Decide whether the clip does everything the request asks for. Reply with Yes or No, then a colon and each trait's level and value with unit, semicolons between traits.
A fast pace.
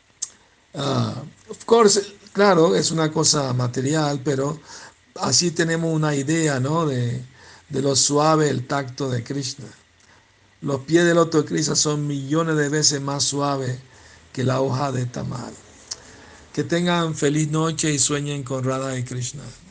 No: average, 145 wpm